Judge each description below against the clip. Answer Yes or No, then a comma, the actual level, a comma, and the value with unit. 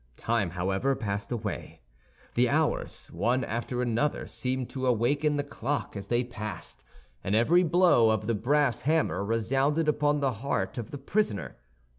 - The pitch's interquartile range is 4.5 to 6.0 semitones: Yes, average, 4.9 semitones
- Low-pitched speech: Yes, low, 125 Hz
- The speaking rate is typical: Yes, average, 155 wpm